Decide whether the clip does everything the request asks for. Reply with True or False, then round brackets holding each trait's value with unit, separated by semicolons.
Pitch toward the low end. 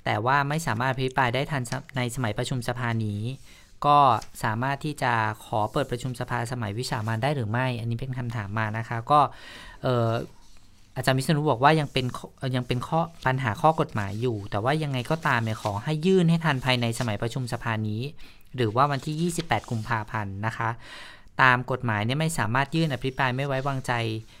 True (125 Hz)